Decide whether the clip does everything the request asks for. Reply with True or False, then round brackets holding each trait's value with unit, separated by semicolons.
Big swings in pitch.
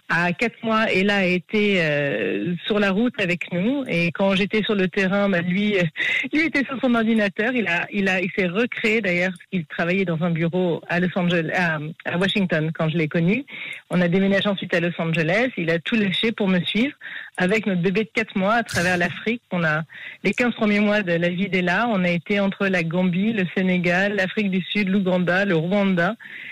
False (3.3 semitones)